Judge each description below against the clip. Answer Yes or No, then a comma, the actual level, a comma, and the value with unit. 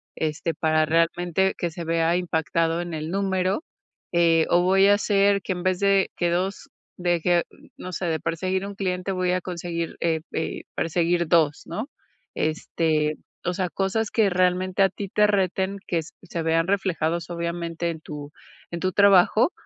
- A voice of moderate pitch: Yes, medium, 175 Hz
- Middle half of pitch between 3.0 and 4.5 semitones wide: No, narrow, 2.4 semitones